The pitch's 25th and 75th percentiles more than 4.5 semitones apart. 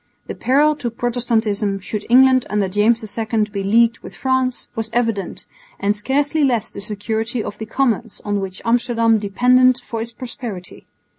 No: average, 3.1 semitones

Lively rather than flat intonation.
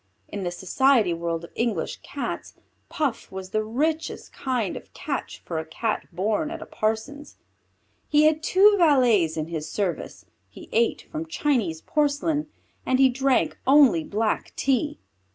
Yes: wide, 7.8 semitones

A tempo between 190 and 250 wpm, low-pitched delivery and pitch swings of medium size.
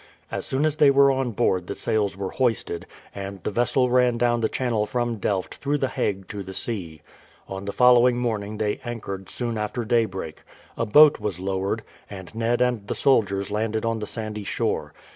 Yes: average, 195 wpm; low, 110 Hz; average, 3.6 semitones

